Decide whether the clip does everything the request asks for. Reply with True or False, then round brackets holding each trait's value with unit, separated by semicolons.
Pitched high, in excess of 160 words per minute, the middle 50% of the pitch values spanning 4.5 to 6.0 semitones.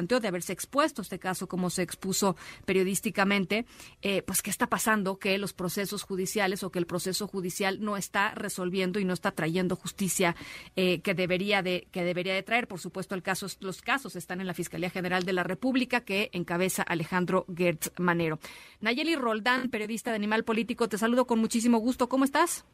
False (195 Hz; 185 wpm; 3.2 semitones)